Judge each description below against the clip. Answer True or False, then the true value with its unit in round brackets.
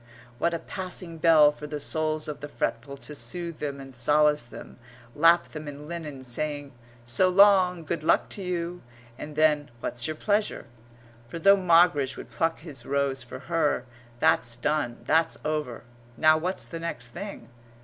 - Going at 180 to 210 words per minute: False (170 wpm)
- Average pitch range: True (3.3 semitones)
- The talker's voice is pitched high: False (155 Hz)